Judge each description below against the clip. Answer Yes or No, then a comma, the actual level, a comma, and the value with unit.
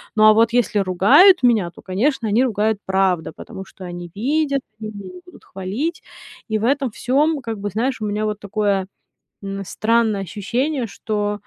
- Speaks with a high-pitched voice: Yes, high, 215 Hz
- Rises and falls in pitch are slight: No, average, 4.1 semitones